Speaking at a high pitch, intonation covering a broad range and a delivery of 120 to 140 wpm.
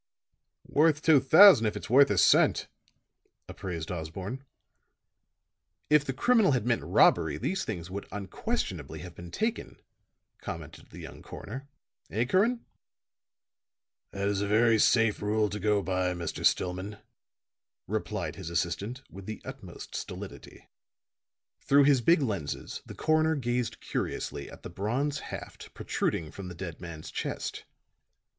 No: low, 105 Hz; wide, 7.3 semitones; slow, 135 wpm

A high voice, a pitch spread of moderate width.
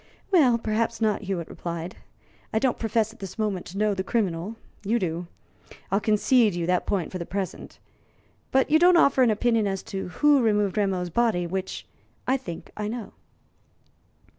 Yes: high, 210 Hz; average, 4.0 semitones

